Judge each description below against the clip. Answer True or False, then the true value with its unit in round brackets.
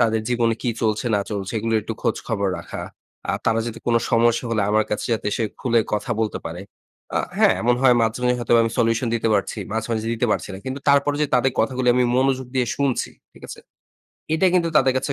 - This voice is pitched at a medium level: False (115 Hz)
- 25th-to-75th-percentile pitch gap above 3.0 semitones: False (2.5 semitones)